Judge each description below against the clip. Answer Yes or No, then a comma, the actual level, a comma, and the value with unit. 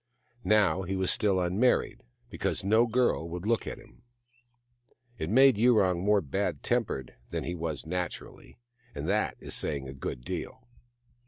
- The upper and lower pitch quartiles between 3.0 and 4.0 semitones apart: No, average, 4.5 semitones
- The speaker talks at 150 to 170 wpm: Yes, average, 155 wpm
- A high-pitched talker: No, very low, 95 Hz